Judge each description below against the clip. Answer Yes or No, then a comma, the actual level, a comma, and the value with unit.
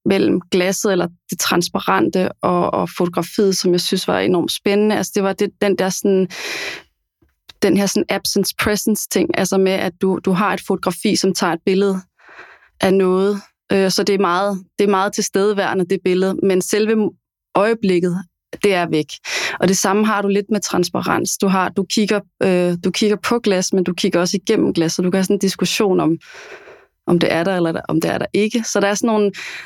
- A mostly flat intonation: Yes, narrow, 1.9 semitones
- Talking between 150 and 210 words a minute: Yes, average, 205 wpm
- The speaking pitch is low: No, high, 195 Hz